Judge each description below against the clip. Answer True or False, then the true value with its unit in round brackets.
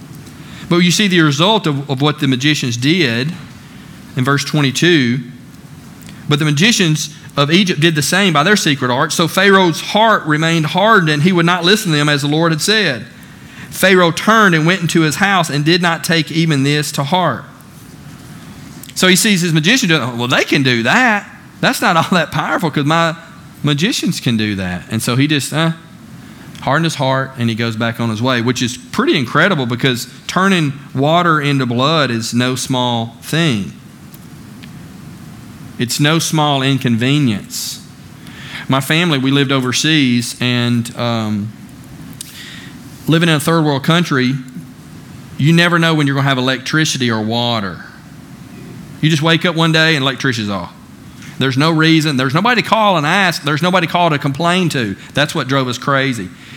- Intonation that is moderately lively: True (4.3 semitones)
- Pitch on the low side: False (150 Hz)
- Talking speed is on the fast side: False (175 wpm)